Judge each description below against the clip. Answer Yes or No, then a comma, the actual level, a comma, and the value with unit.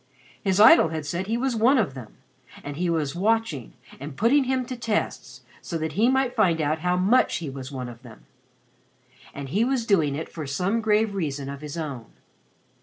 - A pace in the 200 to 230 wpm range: Yes, fast, 205 wpm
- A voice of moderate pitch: Yes, medium, 170 Hz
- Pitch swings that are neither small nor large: No, wide, 7.9 semitones